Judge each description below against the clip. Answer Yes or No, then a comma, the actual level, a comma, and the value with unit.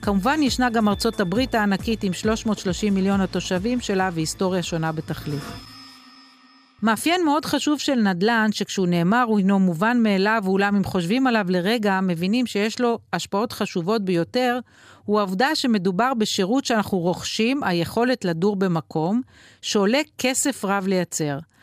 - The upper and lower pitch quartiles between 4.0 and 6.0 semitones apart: Yes, average, 4.4 semitones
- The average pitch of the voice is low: No, high, 210 Hz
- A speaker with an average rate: Yes, average, 135 wpm